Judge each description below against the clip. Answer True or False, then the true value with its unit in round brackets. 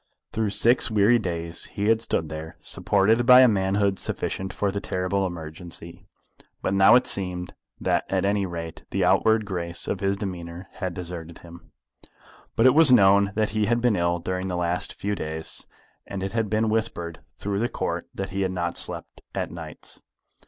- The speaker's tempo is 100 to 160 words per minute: False (185 wpm)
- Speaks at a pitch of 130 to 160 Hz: False (95 Hz)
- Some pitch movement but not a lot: True (3.6 semitones)